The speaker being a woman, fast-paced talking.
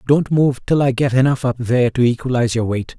No: male; fast, 240 wpm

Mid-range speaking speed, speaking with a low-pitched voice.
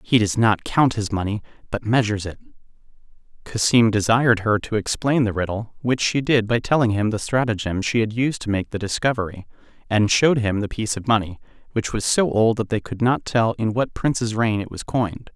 No: fast, 210 wpm; low, 110 Hz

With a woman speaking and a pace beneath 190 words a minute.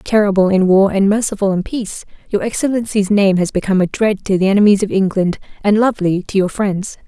No: female; fast, 205 wpm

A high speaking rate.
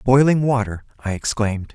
No: average, 140 wpm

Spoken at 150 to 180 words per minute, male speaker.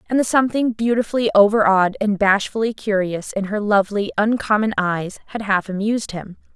No: average, 165 wpm; female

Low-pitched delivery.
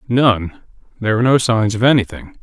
Yes: low, 110 Hz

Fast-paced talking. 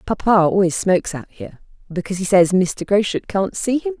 No: average, 195 wpm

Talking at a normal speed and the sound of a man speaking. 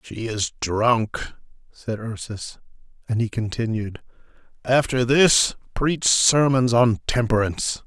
No: slow, 105 wpm; male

